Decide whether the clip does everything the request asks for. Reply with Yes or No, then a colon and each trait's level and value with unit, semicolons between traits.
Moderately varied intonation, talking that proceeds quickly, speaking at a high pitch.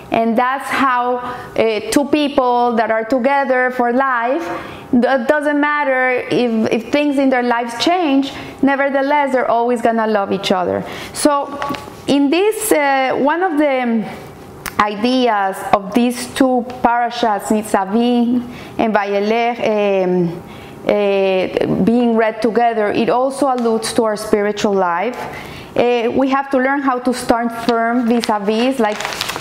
No: average, 3.4 semitones; average, 140 wpm; high, 240 Hz